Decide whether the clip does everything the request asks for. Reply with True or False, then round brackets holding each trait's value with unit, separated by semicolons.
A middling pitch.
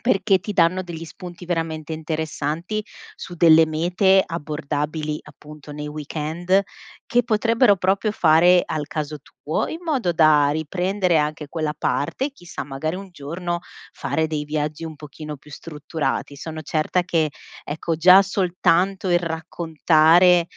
True (165 Hz)